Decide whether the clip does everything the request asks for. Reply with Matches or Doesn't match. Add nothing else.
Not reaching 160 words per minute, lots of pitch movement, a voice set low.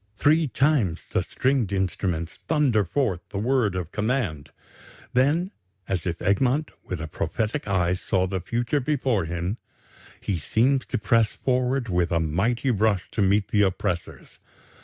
Matches